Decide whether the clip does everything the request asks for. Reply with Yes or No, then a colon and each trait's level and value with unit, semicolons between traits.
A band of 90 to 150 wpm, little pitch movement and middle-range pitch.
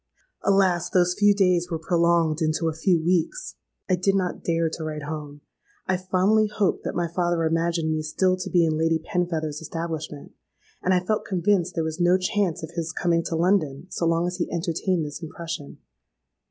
No: average, 190 wpm; narrow, 2.3 semitones; medium, 170 Hz